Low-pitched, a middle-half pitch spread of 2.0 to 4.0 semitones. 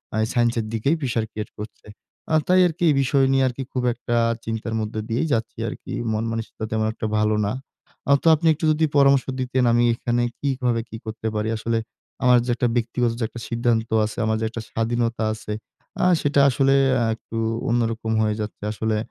Yes: low, 115 Hz; narrow, 2.6 semitones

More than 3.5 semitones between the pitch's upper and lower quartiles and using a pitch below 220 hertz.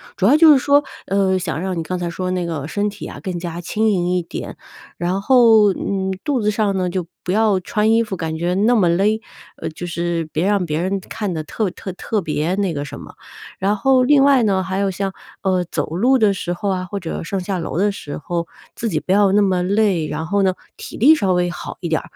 No: average, 3.1 semitones; high, 190 Hz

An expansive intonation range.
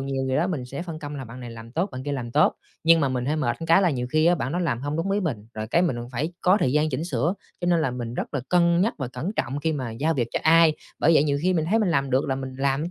No: average, 4.6 semitones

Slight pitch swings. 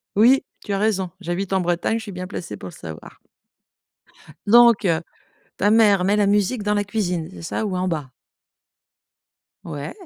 No: average, 3.2 semitones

